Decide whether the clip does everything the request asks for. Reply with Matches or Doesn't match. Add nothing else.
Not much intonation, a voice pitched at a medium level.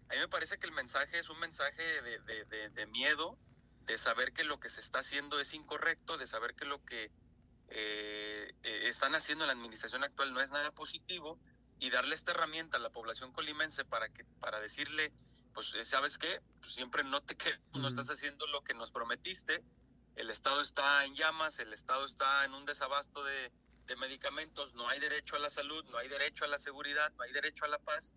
Matches